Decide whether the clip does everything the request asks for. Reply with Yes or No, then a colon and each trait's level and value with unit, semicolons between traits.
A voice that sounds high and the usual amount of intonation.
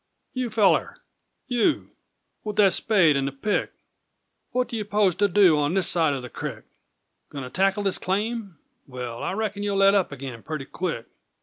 No: high, 195 Hz; wide, 6.3 semitones